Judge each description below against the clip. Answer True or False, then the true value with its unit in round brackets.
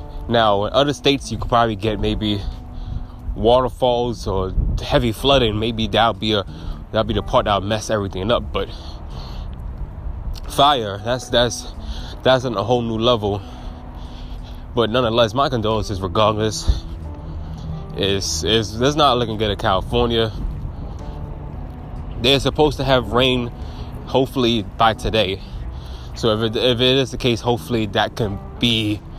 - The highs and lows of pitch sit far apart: True (6.7 semitones)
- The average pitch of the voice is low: True (110 Hz)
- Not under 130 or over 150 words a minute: True (140 wpm)